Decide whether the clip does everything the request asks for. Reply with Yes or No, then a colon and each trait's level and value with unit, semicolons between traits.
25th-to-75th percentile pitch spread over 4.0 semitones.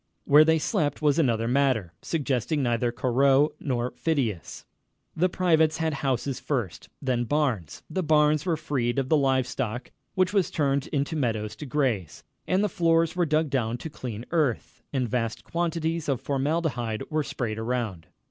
Yes: average, 4.5 semitones